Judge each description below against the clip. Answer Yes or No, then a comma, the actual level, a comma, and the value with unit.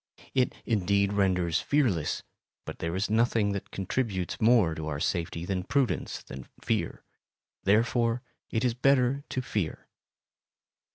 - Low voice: Yes, low, 100 Hz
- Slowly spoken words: Yes, slow, 130 wpm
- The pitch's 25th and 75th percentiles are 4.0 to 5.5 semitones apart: Yes, average, 5.2 semitones